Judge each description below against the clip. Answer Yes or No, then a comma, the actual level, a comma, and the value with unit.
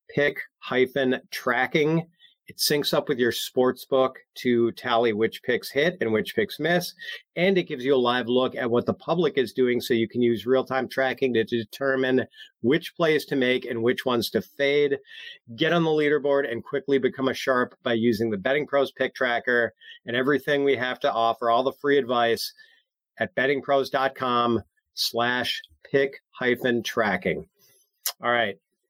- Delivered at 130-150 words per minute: No, average, 170 wpm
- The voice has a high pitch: No, low, 130 Hz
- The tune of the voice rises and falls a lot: No, average, 3.3 semitones